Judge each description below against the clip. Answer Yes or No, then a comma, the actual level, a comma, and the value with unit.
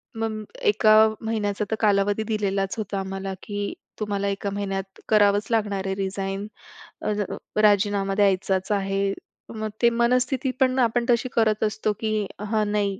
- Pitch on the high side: Yes, high, 205 Hz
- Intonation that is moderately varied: No, narrow, 1.9 semitones